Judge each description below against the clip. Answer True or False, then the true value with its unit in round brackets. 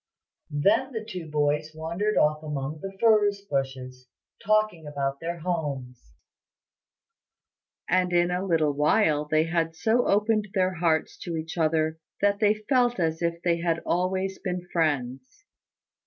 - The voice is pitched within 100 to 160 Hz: False (170 Hz)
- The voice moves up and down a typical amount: True (4.6 semitones)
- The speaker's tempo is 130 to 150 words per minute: True (140 wpm)